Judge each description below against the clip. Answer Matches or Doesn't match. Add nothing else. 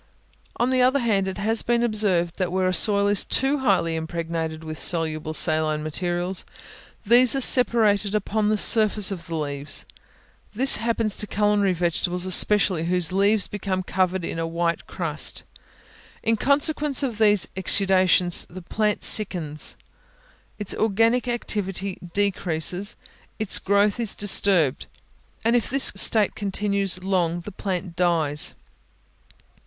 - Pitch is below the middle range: Doesn't match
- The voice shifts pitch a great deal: Doesn't match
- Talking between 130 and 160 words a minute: Matches